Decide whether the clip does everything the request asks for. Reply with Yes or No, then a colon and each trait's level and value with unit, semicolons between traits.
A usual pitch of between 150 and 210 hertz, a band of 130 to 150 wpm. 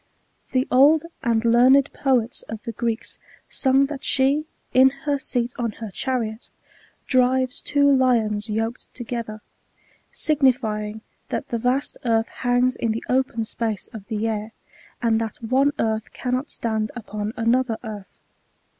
No: high, 235 Hz; average, 145 wpm